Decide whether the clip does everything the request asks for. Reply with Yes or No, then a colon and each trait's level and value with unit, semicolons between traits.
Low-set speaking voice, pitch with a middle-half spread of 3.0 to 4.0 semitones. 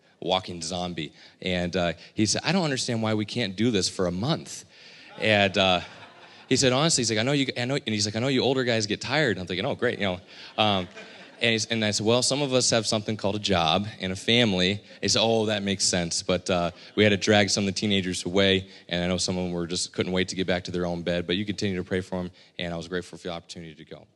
Yes: low, 100 Hz; average, 3.6 semitones